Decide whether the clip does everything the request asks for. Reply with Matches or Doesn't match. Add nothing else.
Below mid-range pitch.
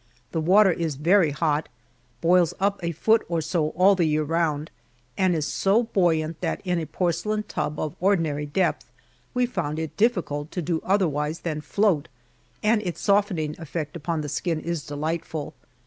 Doesn't match